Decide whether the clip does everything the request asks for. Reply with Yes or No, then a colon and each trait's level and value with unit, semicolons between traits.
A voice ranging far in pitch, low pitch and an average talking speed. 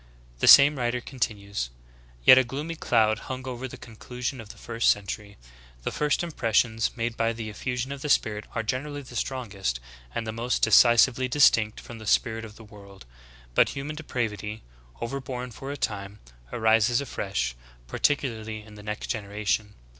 No: average, 3.4 semitones; low, 115 Hz; average, 175 wpm